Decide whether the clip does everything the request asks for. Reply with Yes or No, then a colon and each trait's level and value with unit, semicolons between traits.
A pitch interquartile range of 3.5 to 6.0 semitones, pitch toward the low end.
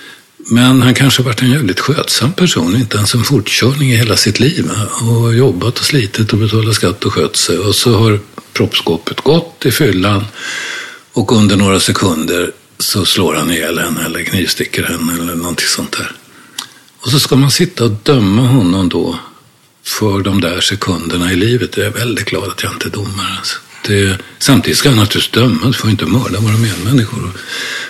Yes: average, 4.2 semitones; low, 115 Hz